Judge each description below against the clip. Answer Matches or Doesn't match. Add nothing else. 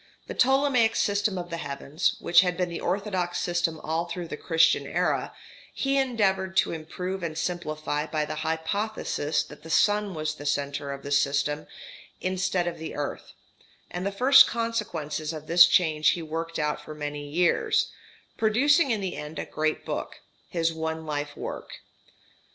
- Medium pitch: Matches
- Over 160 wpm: Matches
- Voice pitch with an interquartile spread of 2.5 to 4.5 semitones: Matches